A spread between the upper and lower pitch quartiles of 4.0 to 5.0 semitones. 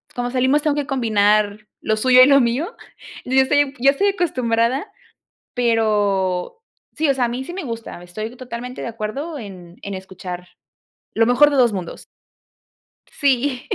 Yes: average, 4.4 semitones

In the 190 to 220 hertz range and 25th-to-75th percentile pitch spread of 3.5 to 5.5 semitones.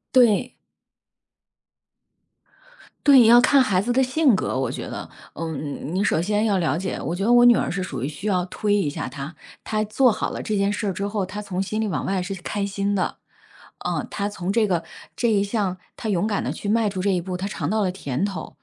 No: high, 200 Hz; average, 2.9 semitones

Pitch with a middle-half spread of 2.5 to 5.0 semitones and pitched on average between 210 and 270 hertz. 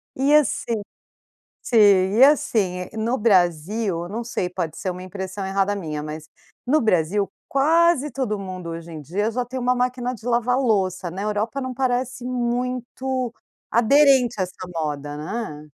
No: wide, 5.4 semitones; high, 215 Hz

